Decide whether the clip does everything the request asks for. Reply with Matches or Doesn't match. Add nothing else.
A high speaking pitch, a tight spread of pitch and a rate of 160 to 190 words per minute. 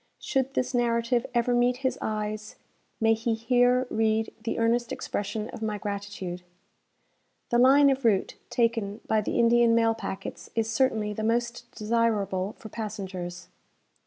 Doesn't match